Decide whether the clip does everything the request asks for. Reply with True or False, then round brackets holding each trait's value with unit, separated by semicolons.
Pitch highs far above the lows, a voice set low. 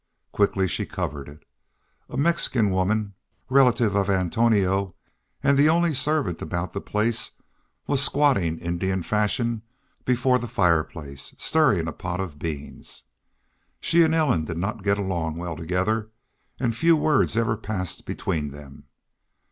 True (6.1 semitones; 100 Hz)